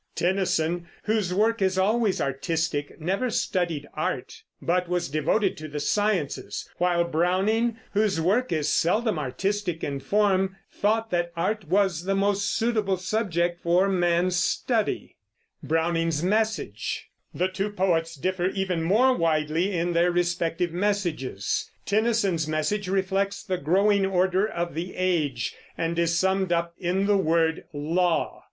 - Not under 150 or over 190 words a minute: No, slow, 135 wpm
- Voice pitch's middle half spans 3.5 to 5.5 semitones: No, average, 3.1 semitones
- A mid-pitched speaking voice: Yes, medium, 180 Hz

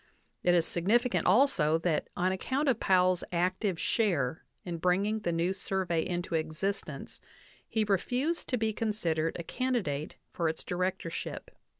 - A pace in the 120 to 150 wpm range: Yes, average, 140 wpm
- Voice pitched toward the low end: No, medium, 185 Hz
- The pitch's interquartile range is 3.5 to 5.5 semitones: Yes, average, 4.4 semitones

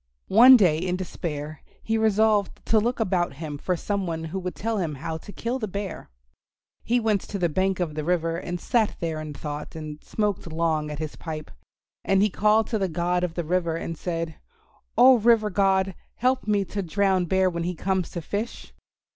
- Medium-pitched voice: Yes, medium, 180 Hz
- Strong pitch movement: No, average, 4.1 semitones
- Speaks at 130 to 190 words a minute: No, fast, 205 wpm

